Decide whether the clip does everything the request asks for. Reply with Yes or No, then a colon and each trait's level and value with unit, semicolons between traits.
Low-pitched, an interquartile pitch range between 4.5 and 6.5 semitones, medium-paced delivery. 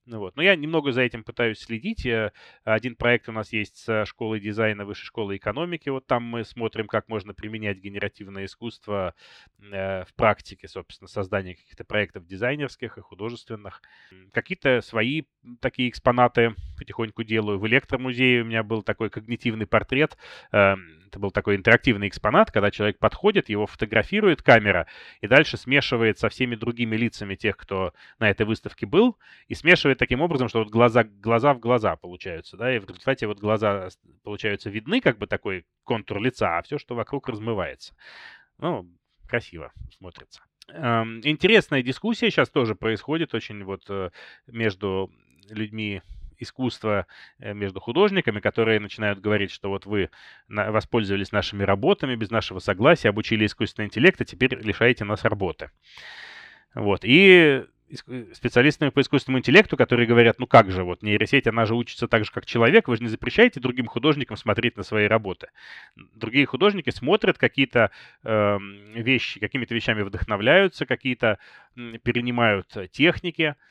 No: low, 115 Hz; average, 3.5 semitones; average, 150 wpm